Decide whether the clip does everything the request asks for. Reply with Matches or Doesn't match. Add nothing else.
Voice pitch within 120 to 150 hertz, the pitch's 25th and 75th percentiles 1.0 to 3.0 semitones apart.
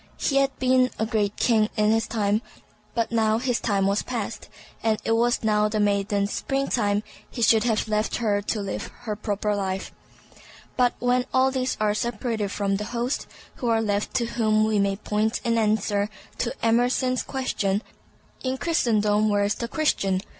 Doesn't match